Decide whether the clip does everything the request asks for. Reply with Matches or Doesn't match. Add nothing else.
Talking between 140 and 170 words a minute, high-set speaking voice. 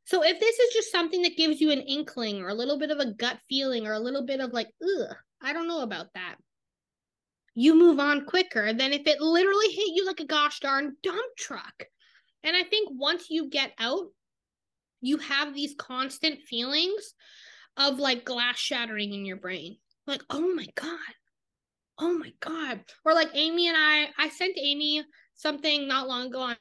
Doesn't match